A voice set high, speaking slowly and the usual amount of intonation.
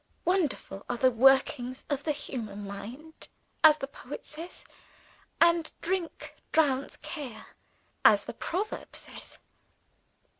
Yes: very high, 280 Hz; slow, 115 wpm; average, 4.5 semitones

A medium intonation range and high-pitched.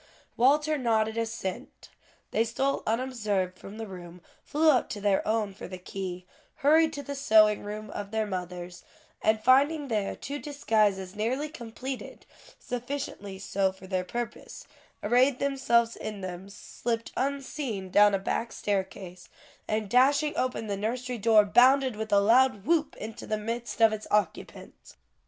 Yes: average, 4.3 semitones; high, 220 Hz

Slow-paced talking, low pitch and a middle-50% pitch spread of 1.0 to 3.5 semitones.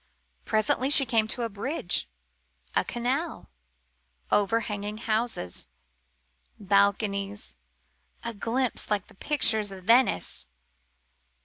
No: slow, 95 wpm; high, 220 Hz; average, 3.0 semitones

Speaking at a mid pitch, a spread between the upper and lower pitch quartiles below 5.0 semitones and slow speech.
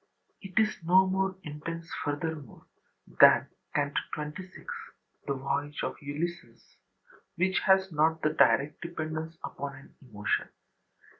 Yes: medium, 160 Hz; average, 3.5 semitones; slow, 120 wpm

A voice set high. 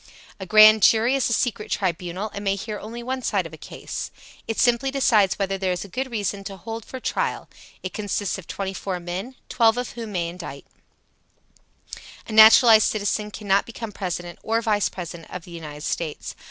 Yes: high, 205 Hz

